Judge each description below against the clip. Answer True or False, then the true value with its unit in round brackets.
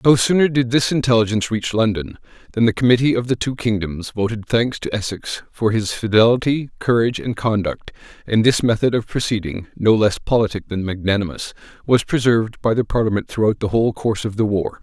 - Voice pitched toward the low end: True (110 Hz)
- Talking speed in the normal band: True (185 wpm)